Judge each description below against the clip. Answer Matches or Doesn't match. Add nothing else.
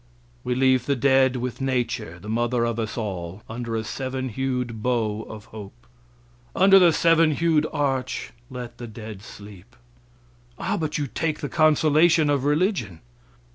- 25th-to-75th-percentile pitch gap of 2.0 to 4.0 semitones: Doesn't match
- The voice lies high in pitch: Doesn't match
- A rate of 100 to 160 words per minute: Matches